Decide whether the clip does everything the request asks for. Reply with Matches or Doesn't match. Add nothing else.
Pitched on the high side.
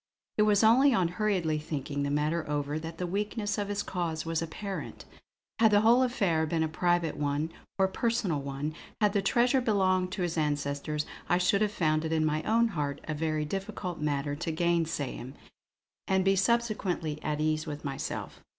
Doesn't match